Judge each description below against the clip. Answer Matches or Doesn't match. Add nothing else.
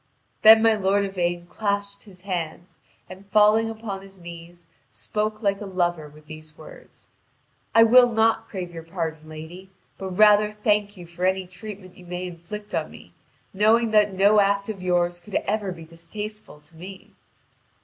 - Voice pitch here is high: Matches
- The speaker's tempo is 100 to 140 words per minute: Doesn't match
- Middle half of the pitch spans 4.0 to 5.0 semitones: Doesn't match